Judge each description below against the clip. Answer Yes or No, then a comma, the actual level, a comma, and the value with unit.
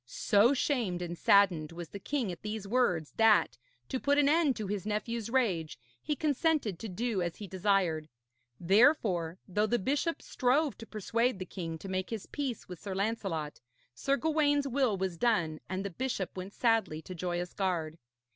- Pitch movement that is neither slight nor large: No, wide, 5.8 semitones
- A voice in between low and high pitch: No, high, 205 Hz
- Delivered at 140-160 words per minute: No, average, 180 wpm